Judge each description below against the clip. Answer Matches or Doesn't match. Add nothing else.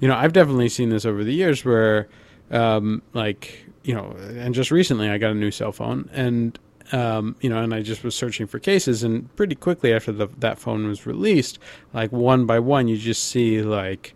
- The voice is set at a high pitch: Doesn't match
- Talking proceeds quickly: Matches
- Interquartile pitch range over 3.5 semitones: Doesn't match